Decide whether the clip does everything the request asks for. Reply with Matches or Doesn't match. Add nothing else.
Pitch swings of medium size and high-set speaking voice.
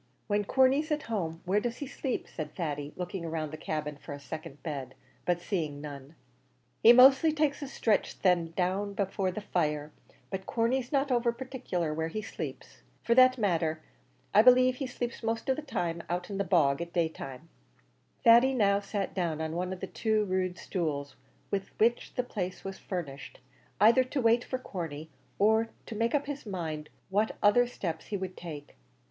Doesn't match